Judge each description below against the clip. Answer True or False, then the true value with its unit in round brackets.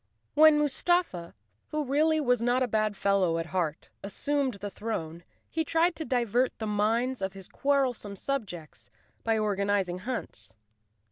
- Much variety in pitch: True (6.1 semitones)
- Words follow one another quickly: False (145 wpm)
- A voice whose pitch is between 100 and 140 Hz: False (225 Hz)